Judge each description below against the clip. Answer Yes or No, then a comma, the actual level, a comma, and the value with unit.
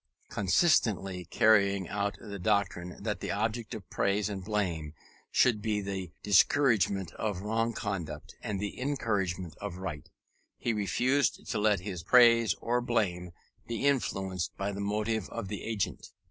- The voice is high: No, low, 100 Hz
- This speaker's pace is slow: No, average, 145 wpm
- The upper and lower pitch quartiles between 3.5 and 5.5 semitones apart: No, average, 3.0 semitones